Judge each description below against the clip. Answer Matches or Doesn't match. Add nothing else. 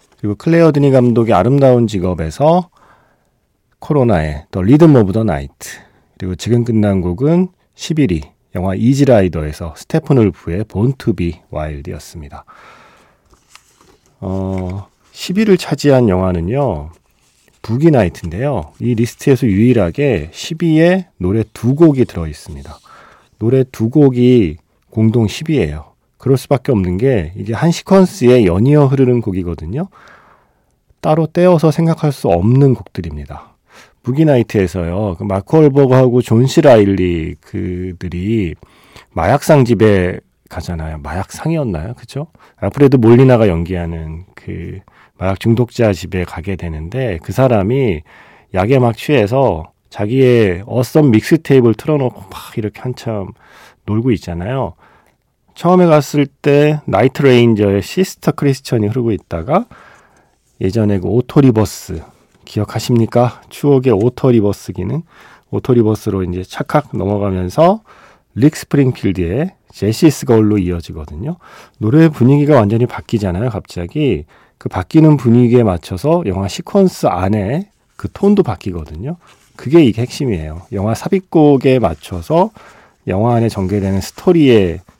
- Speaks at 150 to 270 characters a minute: Doesn't match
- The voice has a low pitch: Matches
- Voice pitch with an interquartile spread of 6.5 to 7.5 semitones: Matches